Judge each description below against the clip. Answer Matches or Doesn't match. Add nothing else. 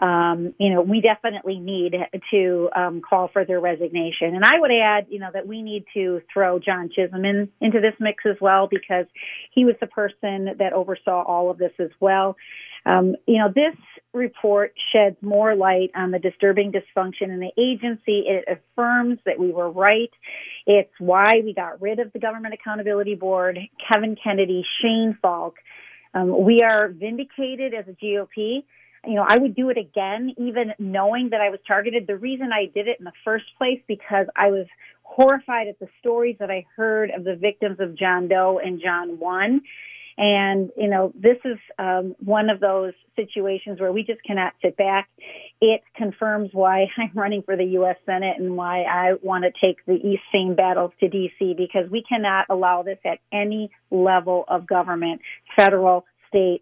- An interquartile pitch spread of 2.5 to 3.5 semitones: Matches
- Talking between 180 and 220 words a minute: Matches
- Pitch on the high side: Matches